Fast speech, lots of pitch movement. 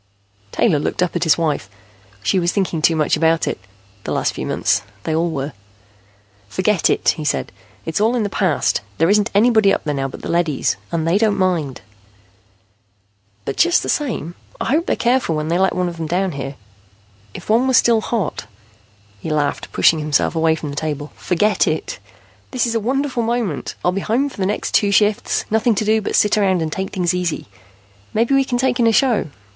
Yes: fast, 210 wpm; wide, 5.8 semitones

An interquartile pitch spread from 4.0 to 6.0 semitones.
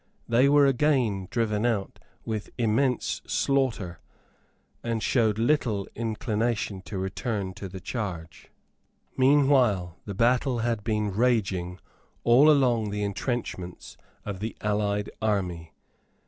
No: average, 3.6 semitones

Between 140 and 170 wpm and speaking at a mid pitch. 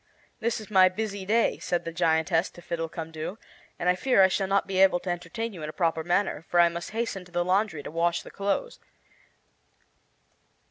No: average, 200 wpm; medium, 180 Hz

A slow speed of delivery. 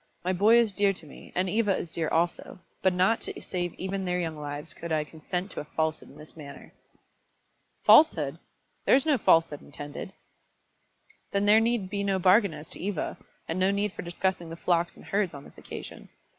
No: average, 200 wpm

